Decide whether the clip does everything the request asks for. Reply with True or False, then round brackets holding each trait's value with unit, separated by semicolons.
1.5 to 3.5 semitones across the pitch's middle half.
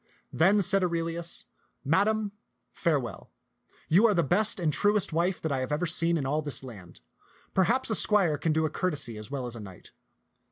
False (5.3 semitones)